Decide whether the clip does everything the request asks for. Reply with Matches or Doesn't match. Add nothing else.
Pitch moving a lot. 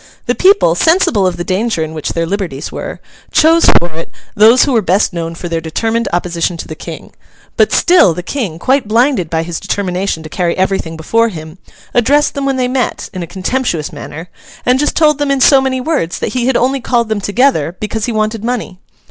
Matches